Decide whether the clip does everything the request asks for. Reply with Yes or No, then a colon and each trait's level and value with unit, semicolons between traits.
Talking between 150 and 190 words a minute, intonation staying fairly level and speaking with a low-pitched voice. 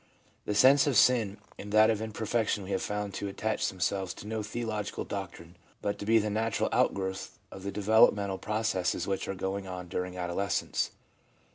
Yes: average, 175 wpm; narrow, 2.3 semitones; low, 100 Hz